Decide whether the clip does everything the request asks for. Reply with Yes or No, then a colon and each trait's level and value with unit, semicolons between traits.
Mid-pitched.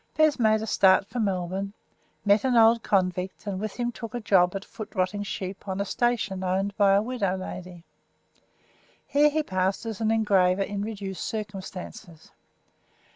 No: high, 200 Hz